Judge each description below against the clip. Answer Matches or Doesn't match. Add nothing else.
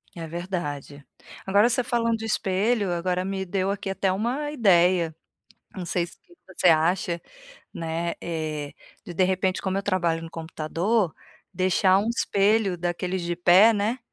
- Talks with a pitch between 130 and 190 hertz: Matches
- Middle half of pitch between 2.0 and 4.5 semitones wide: Matches